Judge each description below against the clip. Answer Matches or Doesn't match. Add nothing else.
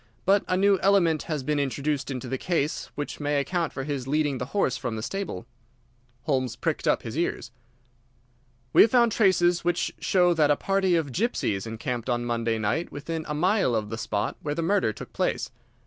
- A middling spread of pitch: Doesn't match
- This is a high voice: Doesn't match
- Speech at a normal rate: Matches